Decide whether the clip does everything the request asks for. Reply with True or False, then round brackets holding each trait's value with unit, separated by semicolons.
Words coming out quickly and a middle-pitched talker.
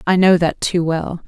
True (235 wpm; 170 Hz)